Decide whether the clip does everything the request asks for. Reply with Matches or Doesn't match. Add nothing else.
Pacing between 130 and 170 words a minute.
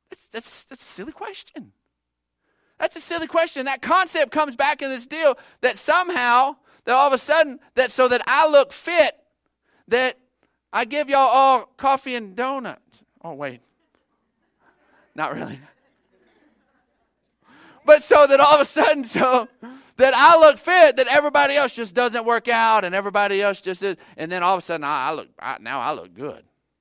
Doesn't match